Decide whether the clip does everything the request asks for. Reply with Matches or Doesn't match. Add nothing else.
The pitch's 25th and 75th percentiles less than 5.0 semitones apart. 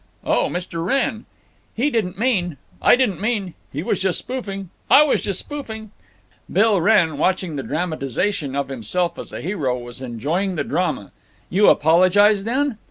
Doesn't match